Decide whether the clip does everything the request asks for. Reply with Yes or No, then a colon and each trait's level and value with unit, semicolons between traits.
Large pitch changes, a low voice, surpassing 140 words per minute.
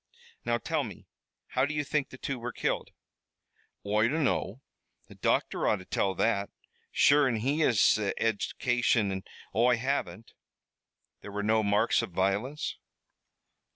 No: average, 4.4 semitones; low, 115 Hz; average, 150 wpm